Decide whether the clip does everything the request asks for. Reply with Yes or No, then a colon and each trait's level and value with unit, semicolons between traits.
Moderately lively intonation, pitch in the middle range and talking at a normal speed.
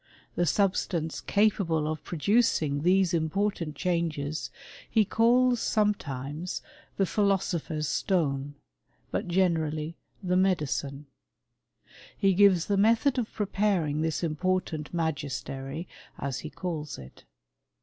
No: average, 4.4 semitones; medium, 170 Hz; slow, 105 wpm